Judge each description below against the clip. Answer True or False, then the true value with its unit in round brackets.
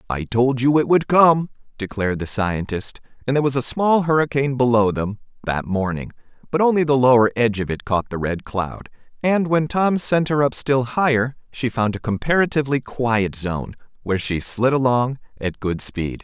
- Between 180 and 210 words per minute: True (190 wpm)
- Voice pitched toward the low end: True (125 Hz)